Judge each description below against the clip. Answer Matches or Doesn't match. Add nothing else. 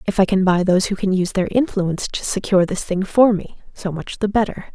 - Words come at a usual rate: Doesn't match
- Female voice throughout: Matches